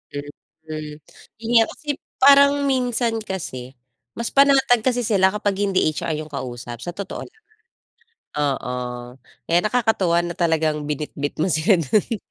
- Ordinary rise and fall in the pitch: No, wide, 7.5 semitones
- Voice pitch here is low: No, medium, 185 Hz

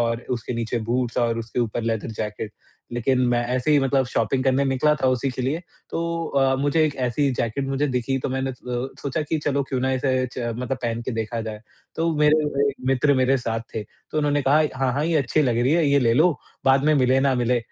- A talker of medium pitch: No, low, 130 Hz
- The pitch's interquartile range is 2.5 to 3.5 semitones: Yes, average, 2.8 semitones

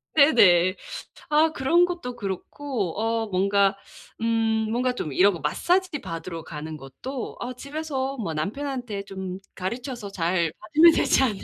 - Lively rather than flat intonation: Yes, wide, 6.8 semitones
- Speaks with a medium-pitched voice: No, high, 220 Hz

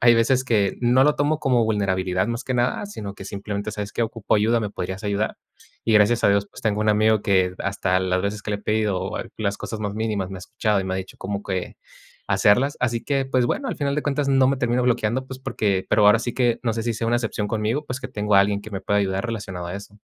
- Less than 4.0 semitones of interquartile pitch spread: Yes, average, 3.2 semitones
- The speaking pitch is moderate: No, low, 110 Hz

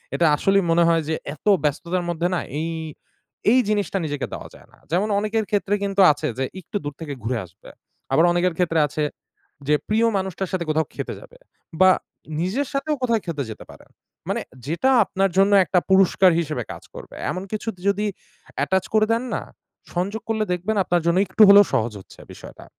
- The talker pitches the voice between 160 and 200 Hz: Yes, medium, 185 Hz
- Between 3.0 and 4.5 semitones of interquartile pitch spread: Yes, average, 4.0 semitones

